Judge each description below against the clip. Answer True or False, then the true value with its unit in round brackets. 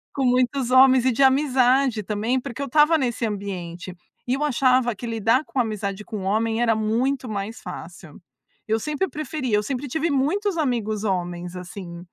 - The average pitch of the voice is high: True (240 Hz)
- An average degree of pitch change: True (4.4 semitones)